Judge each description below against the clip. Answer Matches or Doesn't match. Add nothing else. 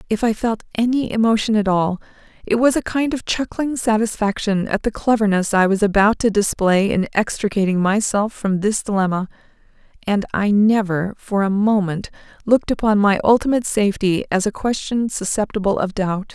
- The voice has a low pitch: Doesn't match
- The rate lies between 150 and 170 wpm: Matches